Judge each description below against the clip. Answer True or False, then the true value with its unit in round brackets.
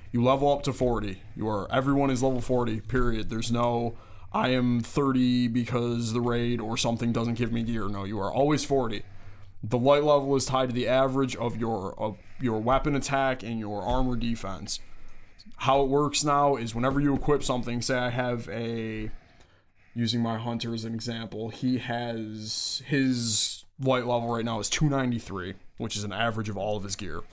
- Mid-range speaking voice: False (120 Hz)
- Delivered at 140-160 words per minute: False (190 wpm)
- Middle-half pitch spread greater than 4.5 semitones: False (3.1 semitones)